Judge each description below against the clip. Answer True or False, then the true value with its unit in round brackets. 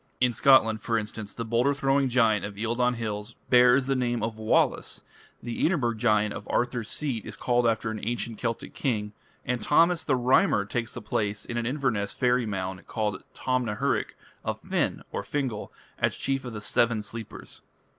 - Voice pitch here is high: False (115 Hz)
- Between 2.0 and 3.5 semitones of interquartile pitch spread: True (2.7 semitones)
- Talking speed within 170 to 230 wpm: True (180 wpm)